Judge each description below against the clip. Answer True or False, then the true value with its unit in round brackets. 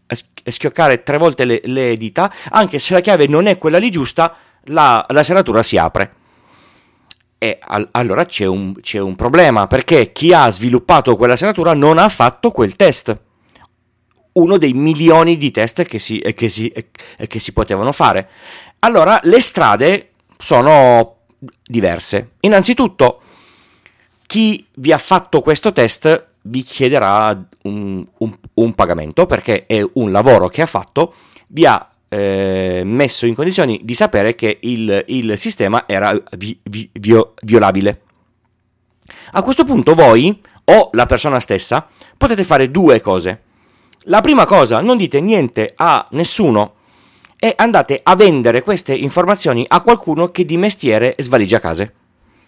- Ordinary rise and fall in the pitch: False (7.6 semitones)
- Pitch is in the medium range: False (125 Hz)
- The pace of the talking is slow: False (145 wpm)